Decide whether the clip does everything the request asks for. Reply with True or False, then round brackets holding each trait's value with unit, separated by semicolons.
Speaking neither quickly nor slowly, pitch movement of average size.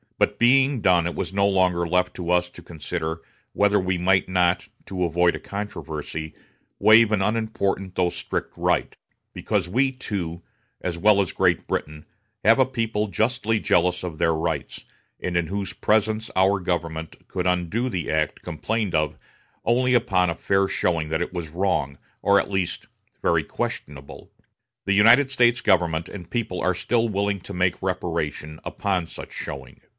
True (170 wpm; 3.6 semitones)